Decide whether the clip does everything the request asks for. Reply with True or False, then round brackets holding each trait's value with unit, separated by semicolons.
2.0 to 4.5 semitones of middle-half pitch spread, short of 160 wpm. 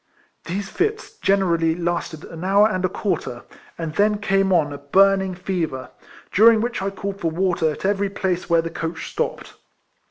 False (3.1 semitones; 170 wpm)